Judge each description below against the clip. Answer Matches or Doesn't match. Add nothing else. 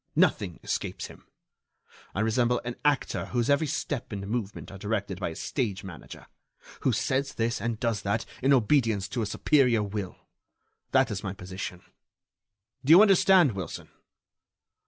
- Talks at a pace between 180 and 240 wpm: Doesn't match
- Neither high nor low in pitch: Doesn't match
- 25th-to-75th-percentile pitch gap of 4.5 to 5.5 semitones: Matches